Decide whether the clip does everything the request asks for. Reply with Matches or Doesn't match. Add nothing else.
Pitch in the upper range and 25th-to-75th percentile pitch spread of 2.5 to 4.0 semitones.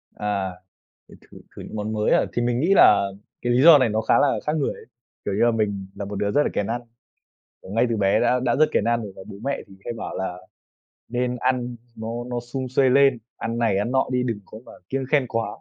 Doesn't match